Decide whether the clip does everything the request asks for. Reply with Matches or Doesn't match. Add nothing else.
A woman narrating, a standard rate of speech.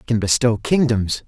Doesn't match